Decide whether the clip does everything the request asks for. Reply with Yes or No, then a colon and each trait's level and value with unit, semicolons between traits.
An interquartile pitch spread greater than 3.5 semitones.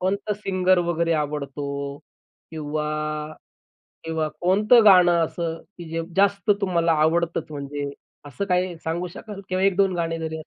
No: average, 3.1 semitones